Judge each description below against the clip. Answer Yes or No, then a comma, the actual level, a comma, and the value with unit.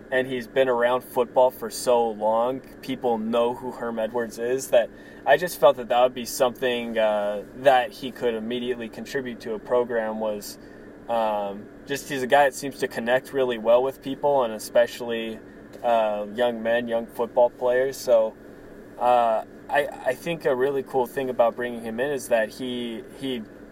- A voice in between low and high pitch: No, low, 120 Hz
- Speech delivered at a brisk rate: No, average, 180 wpm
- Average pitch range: No, narrow, 2.3 semitones